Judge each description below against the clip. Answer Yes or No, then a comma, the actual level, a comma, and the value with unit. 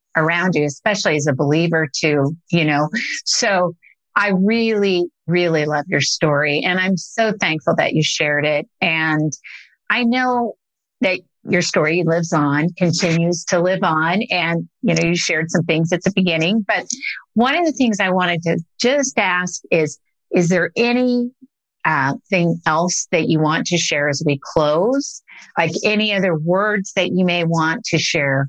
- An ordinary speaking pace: Yes, average, 170 wpm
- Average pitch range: Yes, average, 3.9 semitones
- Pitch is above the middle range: No, medium, 175 Hz